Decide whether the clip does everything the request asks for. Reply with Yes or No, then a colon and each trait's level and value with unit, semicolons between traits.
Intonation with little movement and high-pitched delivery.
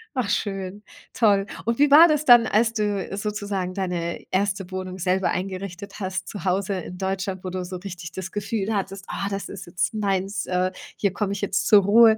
Yes: narrow, 1.9 semitones; high, 195 Hz